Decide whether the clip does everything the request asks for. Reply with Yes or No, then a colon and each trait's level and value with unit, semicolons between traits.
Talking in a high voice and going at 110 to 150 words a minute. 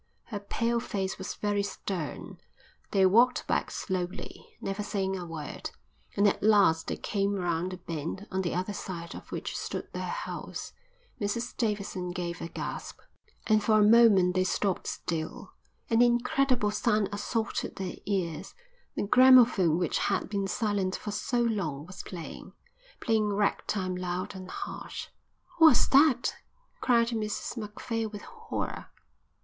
Yes: high, 200 Hz; average, 145 wpm